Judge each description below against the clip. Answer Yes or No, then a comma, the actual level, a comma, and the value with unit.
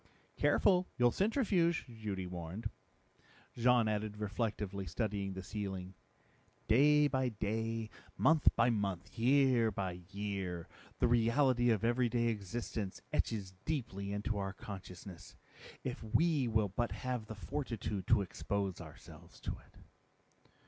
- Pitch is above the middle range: No, low, 110 Hz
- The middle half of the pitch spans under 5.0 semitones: Yes, average, 3.7 semitones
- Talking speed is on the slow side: Yes, slow, 120 wpm